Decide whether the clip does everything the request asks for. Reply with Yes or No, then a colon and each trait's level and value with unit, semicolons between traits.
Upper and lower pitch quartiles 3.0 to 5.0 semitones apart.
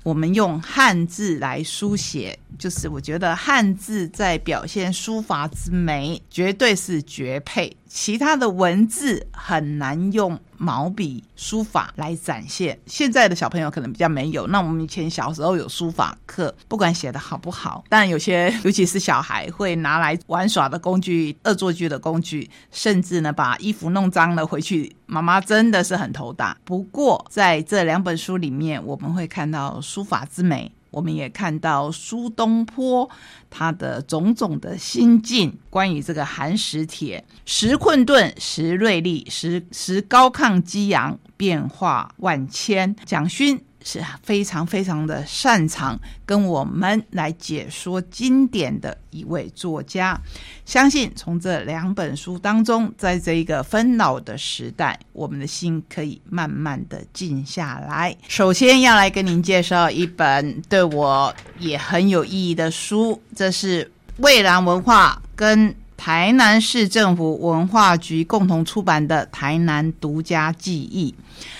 Yes: average, 4.4 semitones